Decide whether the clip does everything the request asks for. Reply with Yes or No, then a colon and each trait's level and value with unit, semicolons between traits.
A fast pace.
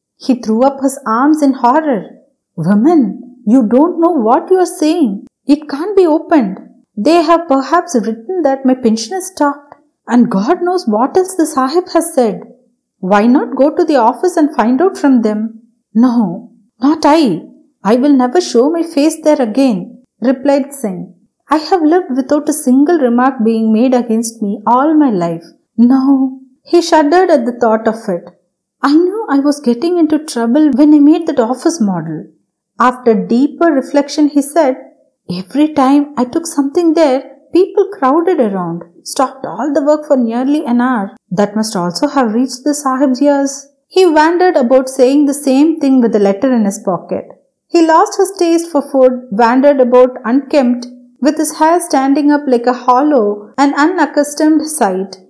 Yes: fast, 175 wpm